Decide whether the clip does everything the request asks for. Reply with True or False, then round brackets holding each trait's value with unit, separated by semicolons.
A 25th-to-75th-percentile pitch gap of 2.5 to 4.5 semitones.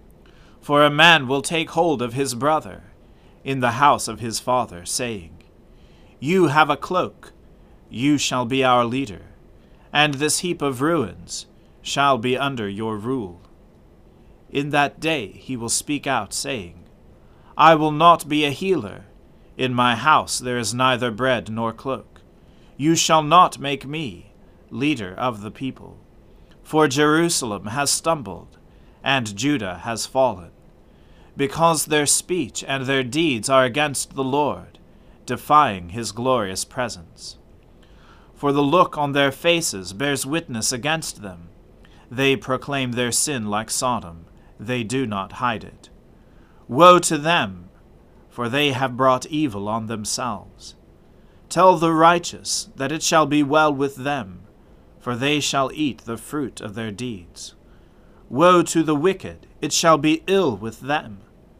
False (5.3 semitones)